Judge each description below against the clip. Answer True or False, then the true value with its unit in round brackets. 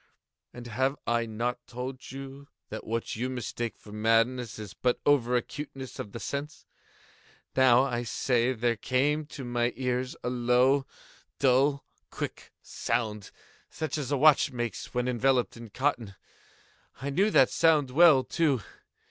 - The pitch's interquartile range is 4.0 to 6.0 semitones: False (2.5 semitones)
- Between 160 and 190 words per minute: False (145 wpm)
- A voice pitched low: True (125 Hz)